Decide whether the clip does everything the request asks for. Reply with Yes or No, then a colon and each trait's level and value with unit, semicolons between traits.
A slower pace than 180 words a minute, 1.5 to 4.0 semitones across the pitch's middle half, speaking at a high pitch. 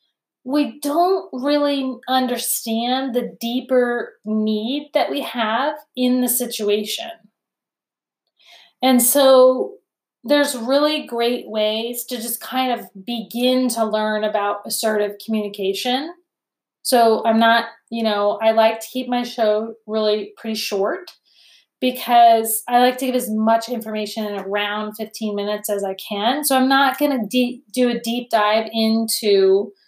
Yes: slow, 135 wpm; average, 3.0 semitones; high, 235 Hz